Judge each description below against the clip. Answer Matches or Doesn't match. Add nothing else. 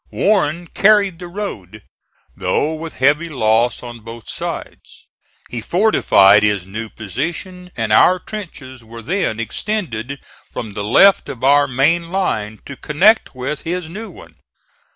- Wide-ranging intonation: Matches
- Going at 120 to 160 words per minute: Matches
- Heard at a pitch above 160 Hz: Doesn't match